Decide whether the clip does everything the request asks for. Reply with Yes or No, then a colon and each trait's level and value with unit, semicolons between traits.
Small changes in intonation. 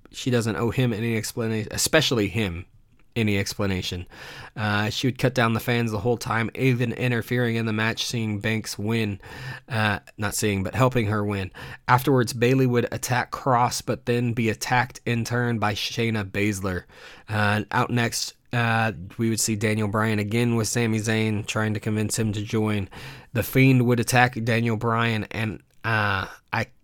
Yes: narrow, 2.3 semitones